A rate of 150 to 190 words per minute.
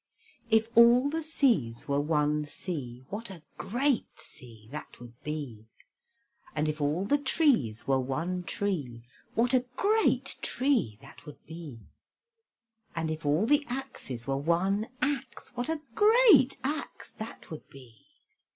No: average, 140 wpm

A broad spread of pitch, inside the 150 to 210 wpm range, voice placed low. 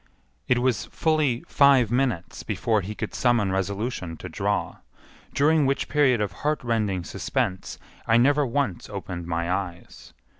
No: wide, 6.0 semitones; average, 140 wpm; low, 115 Hz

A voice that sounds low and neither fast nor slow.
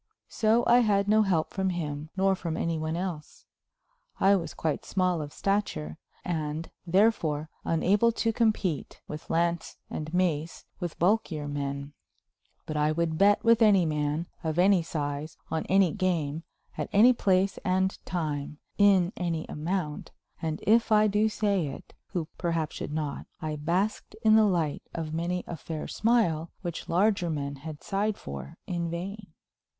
No: medium, 170 Hz; average, 160 wpm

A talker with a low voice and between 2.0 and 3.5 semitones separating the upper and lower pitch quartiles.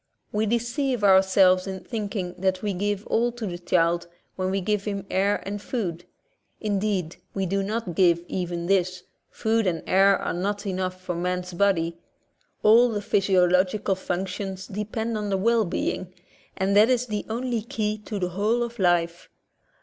No: high, 195 Hz; average, 2.7 semitones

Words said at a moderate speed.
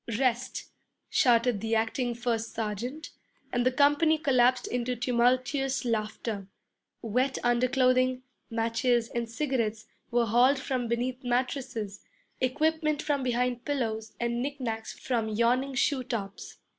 No: slow, 125 wpm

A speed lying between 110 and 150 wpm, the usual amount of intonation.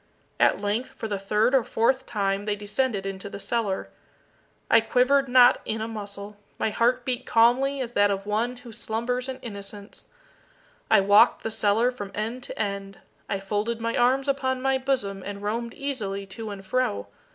No: average, 180 wpm; average, 3.7 semitones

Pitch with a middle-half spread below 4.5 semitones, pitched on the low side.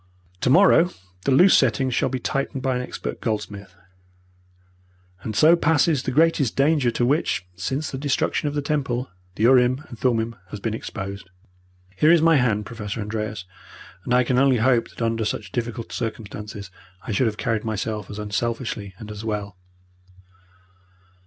Yes: average, 4.1 semitones; low, 120 Hz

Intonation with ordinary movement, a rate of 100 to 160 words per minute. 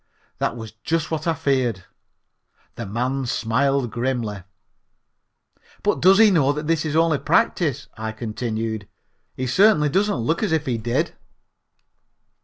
No: wide, 5.8 semitones; average, 140 wpm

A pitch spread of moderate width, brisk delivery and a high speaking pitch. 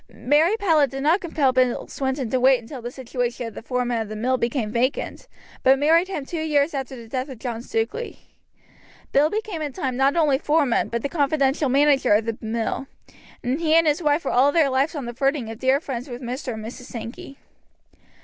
Yes: average, 3.5 semitones; fast, 210 wpm; very high, 265 Hz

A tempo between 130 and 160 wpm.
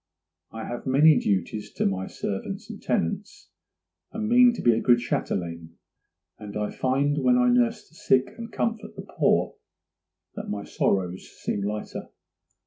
Yes: average, 155 wpm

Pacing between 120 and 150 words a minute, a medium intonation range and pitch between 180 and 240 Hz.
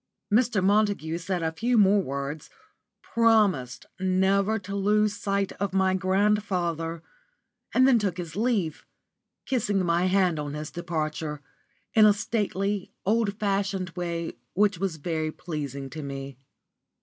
Yes: slow, 135 wpm; average, 4.1 semitones; high, 190 Hz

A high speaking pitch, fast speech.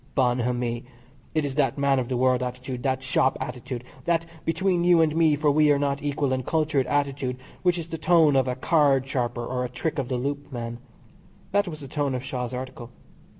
No: low, 135 Hz; fast, 210 wpm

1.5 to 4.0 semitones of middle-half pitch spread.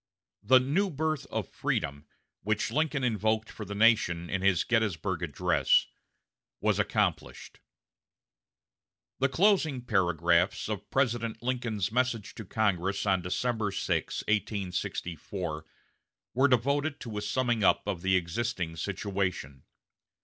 No: average, 5.1 semitones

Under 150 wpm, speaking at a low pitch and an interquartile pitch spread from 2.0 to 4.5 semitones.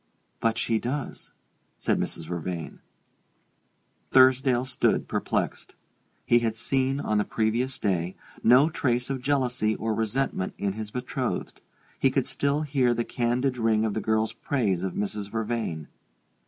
Yes: average, 140 wpm; low, 115 Hz; average, 3.4 semitones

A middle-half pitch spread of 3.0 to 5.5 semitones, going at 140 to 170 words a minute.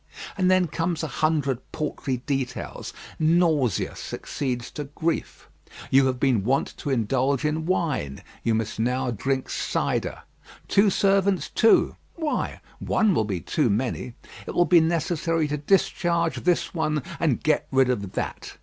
Yes: average, 4.9 semitones; average, 150 wpm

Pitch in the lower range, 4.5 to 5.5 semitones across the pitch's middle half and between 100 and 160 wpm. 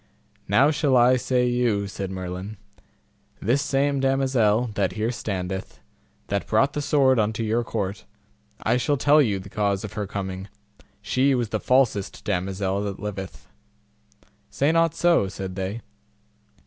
Yes: low, 110 Hz; average, 5.2 semitones; average, 150 wpm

